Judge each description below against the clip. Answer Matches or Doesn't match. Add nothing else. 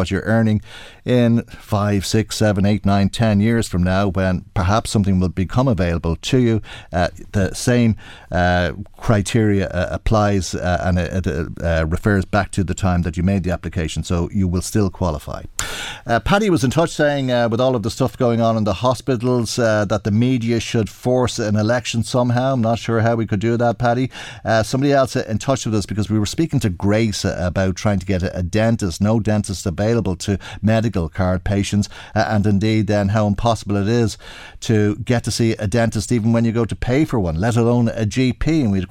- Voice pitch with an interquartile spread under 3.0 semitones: Doesn't match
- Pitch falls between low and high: Doesn't match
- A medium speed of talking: Doesn't match